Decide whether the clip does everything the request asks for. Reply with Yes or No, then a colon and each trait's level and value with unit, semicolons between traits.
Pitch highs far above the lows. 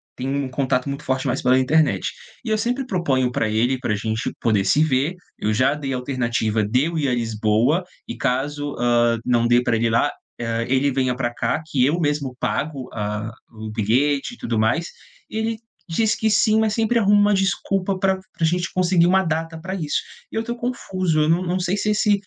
Yes: wide, 7.3 semitones